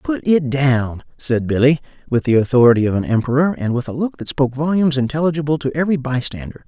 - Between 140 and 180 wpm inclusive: No, fast, 205 wpm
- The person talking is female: No, male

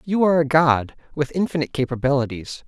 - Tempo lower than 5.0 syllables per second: No, 6.3 syllables/s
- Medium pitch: Yes, medium, 145 Hz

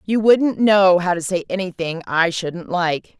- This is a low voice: No, medium, 185 Hz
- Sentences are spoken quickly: No, average, 190 wpm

